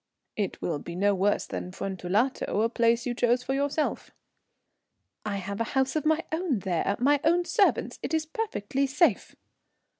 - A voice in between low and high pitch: No, high, 240 Hz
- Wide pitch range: Yes, wide, 6.8 semitones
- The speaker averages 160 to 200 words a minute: Yes, average, 170 wpm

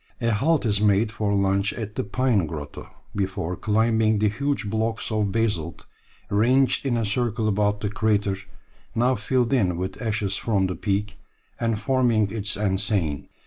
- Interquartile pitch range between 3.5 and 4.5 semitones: No, narrow, 2.5 semitones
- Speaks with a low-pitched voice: Yes, low, 105 Hz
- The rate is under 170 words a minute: Yes, average, 160 wpm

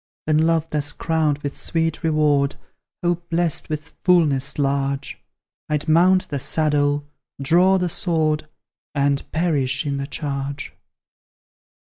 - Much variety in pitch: No, narrow, 2.5 semitones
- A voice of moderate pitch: Yes, medium, 150 Hz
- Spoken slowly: Yes, slow, 120 wpm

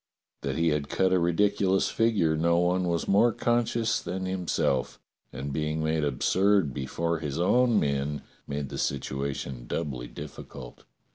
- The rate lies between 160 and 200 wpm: No, average, 145 wpm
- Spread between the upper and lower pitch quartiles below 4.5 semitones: No, average, 5.1 semitones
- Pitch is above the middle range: No, very low, 85 Hz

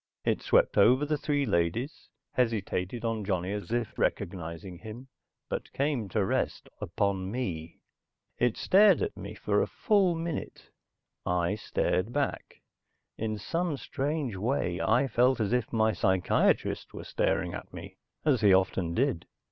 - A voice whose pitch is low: Yes, low, 110 Hz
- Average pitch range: No, wide, 6.4 semitones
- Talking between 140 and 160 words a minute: Yes, average, 150 wpm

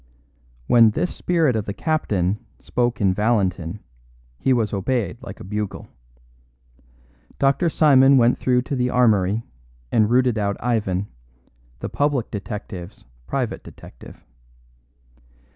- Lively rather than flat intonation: No, average, 4.1 semitones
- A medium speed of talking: No, slow, 120 wpm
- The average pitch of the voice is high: No, low, 115 Hz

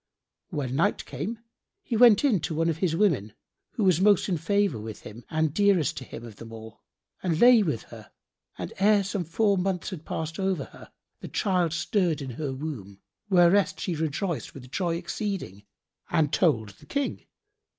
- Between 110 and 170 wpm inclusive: No, average, 180 wpm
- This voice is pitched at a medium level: Yes, medium, 165 Hz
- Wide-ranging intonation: Yes, wide, 6.4 semitones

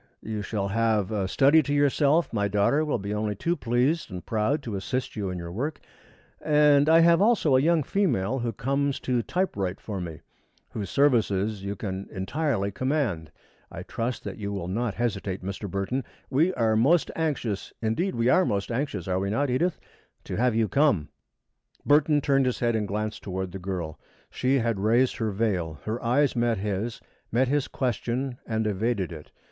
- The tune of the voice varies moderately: No, wide, 5.7 semitones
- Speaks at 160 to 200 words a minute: Yes, average, 185 wpm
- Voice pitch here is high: No, low, 115 Hz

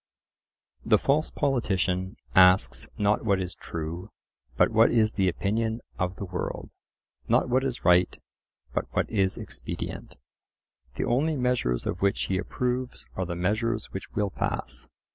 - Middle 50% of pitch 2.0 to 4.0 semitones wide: No, average, 4.4 semitones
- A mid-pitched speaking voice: No, low, 100 Hz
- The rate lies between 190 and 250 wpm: No, average, 145 wpm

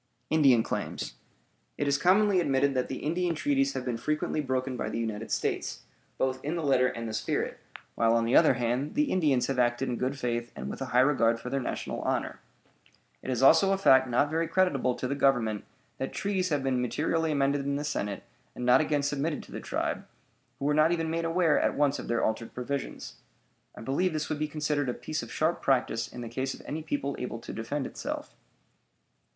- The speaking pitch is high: No, medium, 140 Hz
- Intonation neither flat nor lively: Yes, average, 3.8 semitones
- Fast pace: Yes, fast, 215 wpm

